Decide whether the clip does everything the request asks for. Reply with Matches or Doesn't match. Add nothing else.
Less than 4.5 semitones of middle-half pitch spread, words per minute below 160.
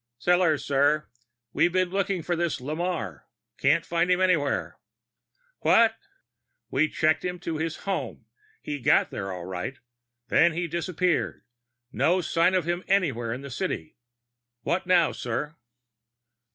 Matches